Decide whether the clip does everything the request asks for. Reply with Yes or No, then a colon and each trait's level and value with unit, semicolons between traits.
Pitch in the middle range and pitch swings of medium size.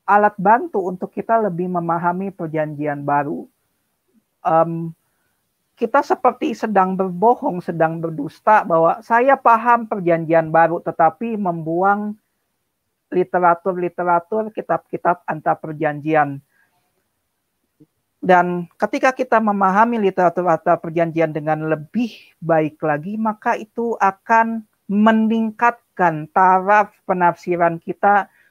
Yes: medium, 180 Hz; average, 4.9 semitones